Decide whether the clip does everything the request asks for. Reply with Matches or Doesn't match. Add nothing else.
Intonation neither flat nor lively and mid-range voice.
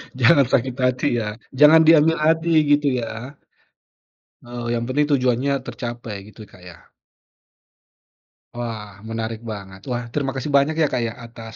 Doesn't match